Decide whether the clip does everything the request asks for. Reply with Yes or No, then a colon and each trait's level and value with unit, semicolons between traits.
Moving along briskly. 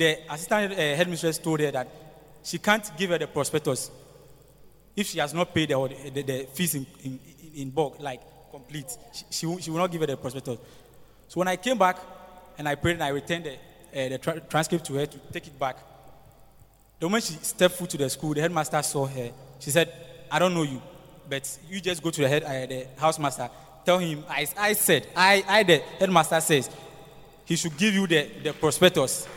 Yes: fast, 215 wpm